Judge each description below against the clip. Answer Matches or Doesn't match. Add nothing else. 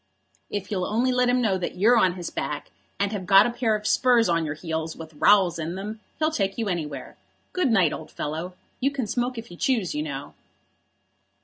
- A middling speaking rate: Doesn't match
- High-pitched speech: Matches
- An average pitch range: Doesn't match